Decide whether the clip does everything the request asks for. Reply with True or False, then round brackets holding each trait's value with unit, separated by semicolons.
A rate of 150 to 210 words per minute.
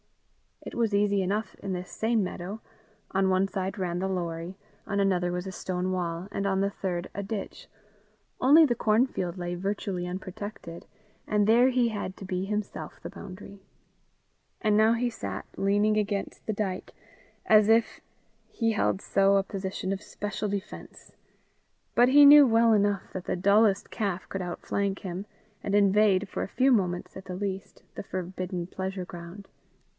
True (170 wpm)